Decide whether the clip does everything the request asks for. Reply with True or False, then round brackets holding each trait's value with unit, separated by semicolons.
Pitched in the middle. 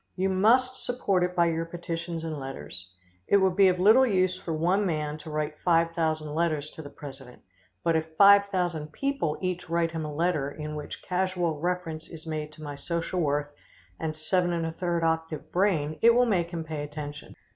True (165 Hz)